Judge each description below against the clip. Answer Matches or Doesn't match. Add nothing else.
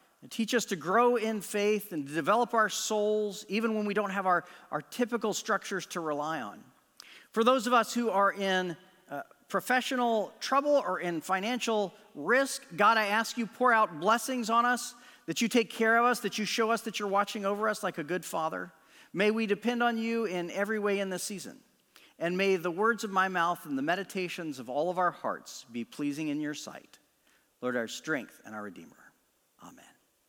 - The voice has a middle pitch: Doesn't match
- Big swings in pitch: Doesn't match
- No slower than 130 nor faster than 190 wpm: Doesn't match